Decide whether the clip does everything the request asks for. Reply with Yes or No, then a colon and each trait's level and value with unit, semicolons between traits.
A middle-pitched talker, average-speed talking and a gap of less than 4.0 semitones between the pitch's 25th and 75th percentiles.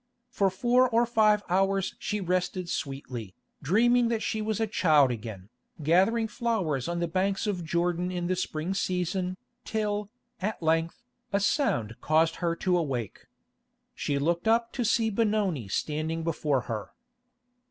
No: medium, 180 Hz; average, 150 wpm; average, 5.2 semitones